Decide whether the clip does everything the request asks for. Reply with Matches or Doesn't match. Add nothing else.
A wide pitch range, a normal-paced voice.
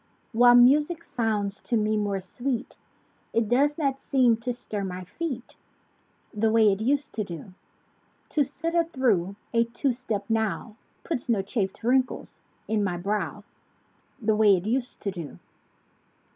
Doesn't match